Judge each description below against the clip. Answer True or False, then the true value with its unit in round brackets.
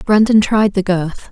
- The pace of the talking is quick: False (180 wpm)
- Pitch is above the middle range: True (200 Hz)